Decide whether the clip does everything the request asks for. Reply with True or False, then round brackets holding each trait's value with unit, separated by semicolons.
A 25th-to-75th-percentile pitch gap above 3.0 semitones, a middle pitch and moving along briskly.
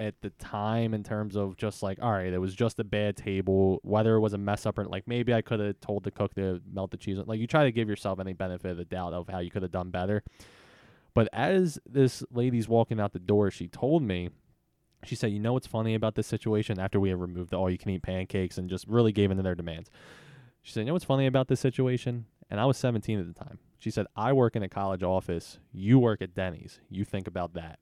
False (3.5 semitones; 105 Hz; 265 wpm)